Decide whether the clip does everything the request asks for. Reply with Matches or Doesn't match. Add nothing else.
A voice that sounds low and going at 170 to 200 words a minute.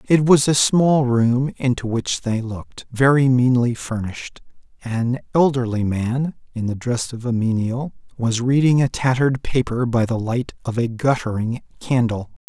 Doesn't match